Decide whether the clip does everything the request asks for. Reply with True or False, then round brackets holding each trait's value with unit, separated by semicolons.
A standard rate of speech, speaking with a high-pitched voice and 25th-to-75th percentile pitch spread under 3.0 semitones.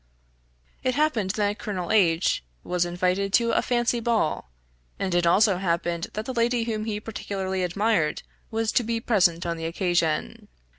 False (160 wpm; 195 Hz; 4.4 semitones)